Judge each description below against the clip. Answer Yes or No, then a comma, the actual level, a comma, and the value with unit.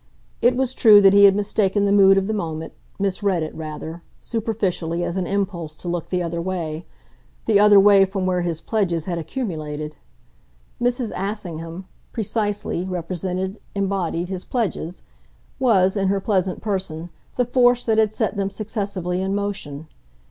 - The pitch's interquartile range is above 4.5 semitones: No, average, 3.2 semitones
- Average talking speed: Yes, average, 160 wpm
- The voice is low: No, high, 190 Hz